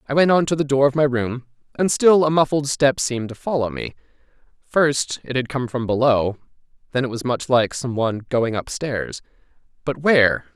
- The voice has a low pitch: Yes, low, 130 Hz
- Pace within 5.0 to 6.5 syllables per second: Yes, 5.2 syllables/s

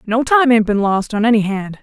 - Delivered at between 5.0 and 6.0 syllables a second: Yes, 5.3 syllables/s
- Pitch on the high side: Yes, high, 225 Hz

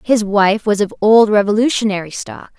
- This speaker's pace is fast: No, average, 160 wpm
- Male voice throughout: No, female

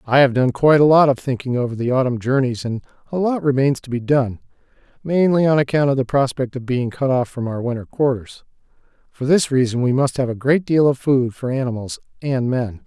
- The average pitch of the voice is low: Yes, low, 130 Hz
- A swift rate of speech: Yes, fast, 225 wpm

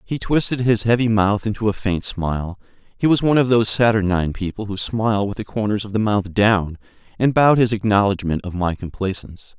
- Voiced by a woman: No, male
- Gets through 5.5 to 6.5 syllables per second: Yes, 5.9 syllables/s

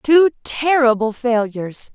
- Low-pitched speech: No, very high, 250 Hz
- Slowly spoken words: Yes, slow, 90 wpm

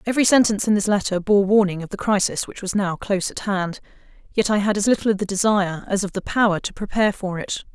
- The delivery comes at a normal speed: No, fast, 250 wpm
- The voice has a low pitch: No, high, 200 Hz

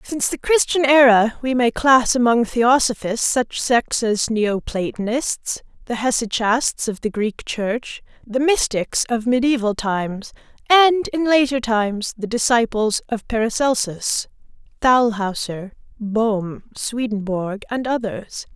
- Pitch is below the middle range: No, high, 235 Hz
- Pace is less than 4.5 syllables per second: Yes, 4.0 syllables/s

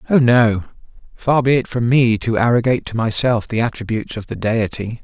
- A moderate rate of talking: Yes, average, 190 wpm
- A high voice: No, low, 115 Hz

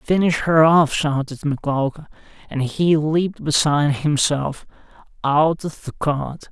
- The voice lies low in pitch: No, medium, 150 Hz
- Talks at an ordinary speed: No, slow, 130 wpm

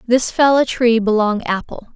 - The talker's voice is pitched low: No, high, 235 Hz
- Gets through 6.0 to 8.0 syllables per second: No, 4.6 syllables/s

